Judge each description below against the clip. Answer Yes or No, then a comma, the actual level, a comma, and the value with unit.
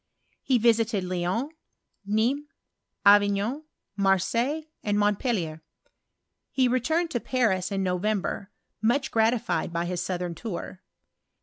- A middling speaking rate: No, slow, 105 wpm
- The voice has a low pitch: No, high, 210 Hz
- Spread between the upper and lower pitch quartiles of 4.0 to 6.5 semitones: Yes, average, 4.5 semitones